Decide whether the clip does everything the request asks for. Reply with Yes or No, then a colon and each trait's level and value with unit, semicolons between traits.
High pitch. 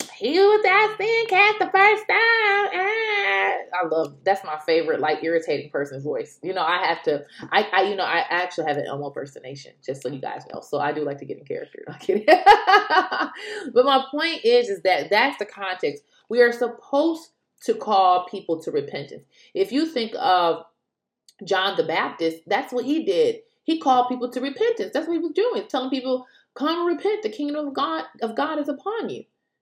Yes: very high, 300 Hz